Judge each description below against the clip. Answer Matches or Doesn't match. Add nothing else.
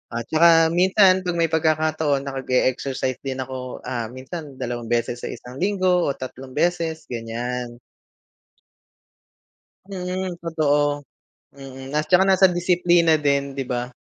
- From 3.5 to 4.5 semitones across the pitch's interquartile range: Doesn't match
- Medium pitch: Matches